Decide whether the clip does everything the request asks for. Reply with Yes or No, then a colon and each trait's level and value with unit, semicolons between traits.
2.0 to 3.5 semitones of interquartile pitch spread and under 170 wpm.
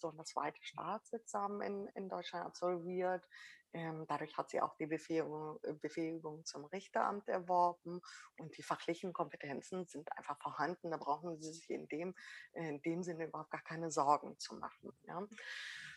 Yes: average, 2.8 semitones; average, 160 wpm